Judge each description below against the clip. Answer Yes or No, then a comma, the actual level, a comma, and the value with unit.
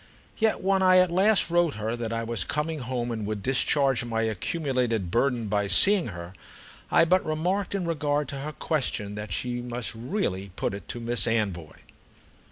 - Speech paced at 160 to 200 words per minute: Yes, average, 180 wpm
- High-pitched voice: No, low, 125 Hz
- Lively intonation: Yes, wide, 6.8 semitones